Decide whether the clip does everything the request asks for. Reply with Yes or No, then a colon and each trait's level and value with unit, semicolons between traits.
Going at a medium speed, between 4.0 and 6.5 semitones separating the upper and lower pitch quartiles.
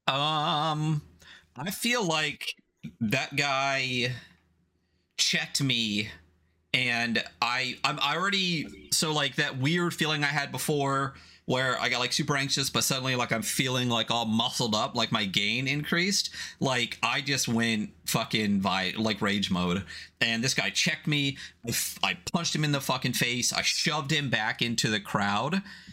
Yes: average, 160 wpm; wide, 5.4 semitones